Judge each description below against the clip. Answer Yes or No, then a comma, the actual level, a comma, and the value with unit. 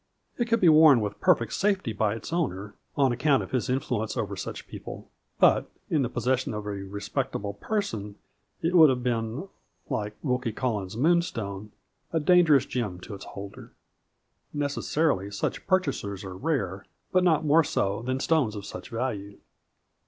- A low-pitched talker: Yes, low, 125 Hz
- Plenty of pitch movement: Yes, wide, 7.1 semitones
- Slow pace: No, average, 160 wpm